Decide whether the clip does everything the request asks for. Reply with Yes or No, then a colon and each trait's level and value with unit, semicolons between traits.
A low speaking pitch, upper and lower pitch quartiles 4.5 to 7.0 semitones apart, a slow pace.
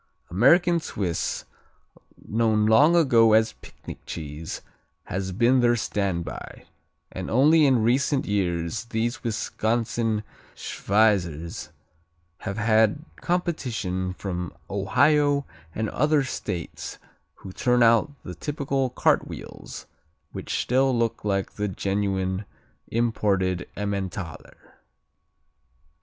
Yes: low, 110 Hz; average, 5.0 semitones; slow, 95 wpm